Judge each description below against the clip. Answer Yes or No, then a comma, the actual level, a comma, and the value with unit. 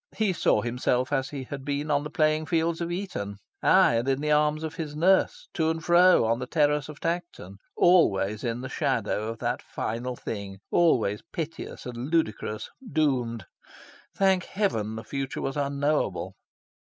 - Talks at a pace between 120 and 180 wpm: Yes, average, 170 wpm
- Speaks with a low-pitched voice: No, medium, 145 Hz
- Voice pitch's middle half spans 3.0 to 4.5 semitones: No, wide, 5.6 semitones